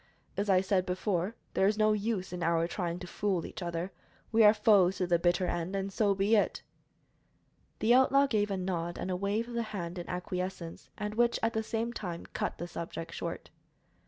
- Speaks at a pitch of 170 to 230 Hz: Yes, high, 190 Hz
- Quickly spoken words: Yes, fast, 210 wpm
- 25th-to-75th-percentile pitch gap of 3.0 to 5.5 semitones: Yes, average, 3.4 semitones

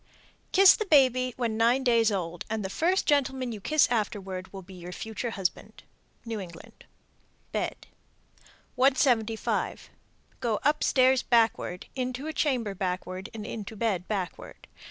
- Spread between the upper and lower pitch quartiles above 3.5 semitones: Yes, average, 4.9 semitones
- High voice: Yes, high, 225 Hz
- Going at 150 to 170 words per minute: No, slow, 135 wpm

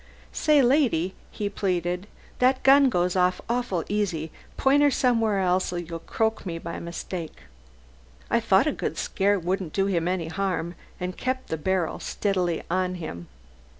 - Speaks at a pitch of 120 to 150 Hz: No, medium, 185 Hz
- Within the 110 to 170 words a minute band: Yes, average, 160 wpm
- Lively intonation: No, average, 4.2 semitones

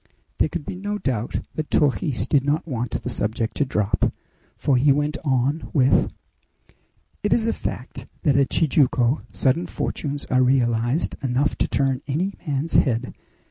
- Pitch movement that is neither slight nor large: Yes, average, 3.4 semitones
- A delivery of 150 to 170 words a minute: Yes, average, 160 wpm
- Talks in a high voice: No, medium, 140 Hz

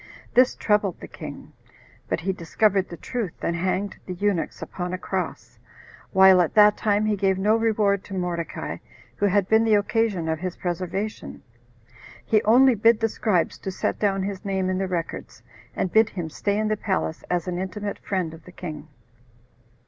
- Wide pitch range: No, average, 2.7 semitones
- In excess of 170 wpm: Yes, average, 185 wpm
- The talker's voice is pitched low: No, high, 195 Hz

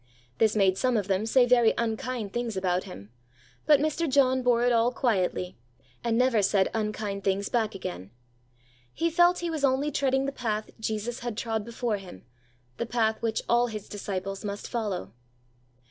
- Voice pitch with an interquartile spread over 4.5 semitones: No, average, 3.8 semitones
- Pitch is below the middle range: No, high, 225 Hz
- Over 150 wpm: Yes, average, 175 wpm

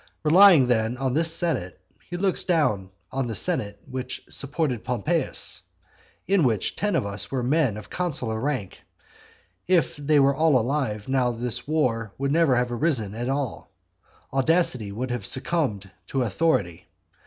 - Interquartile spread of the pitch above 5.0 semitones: Yes, wide, 5.6 semitones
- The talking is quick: No, average, 155 wpm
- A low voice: Yes, low, 130 Hz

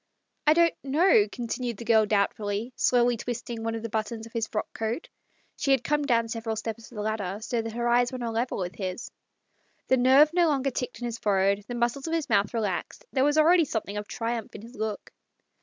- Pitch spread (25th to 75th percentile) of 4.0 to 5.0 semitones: No, average, 2.9 semitones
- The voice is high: Yes, high, 230 Hz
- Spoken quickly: Yes, fast, 235 wpm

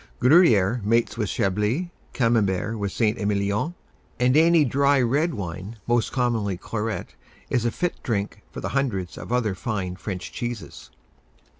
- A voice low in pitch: Yes, low, 115 Hz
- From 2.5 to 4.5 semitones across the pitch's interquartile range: Yes, average, 3.8 semitones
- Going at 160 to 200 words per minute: No, average, 145 wpm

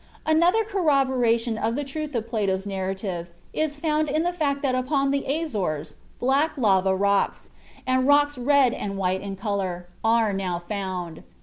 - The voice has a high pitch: Yes, high, 235 Hz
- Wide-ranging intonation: Yes, wide, 6.9 semitones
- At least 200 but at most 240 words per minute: No, average, 160 wpm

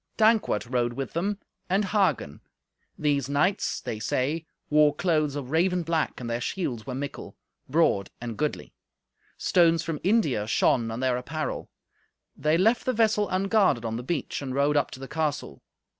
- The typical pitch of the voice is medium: Yes, medium, 150 Hz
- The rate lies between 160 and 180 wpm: Yes, average, 165 wpm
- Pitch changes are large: Yes, wide, 6.0 semitones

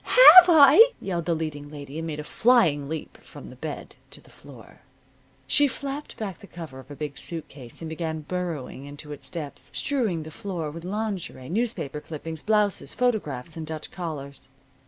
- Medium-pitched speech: Yes, medium, 165 Hz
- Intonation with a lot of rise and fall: Yes, wide, 6.0 semitones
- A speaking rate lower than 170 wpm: No, average, 180 wpm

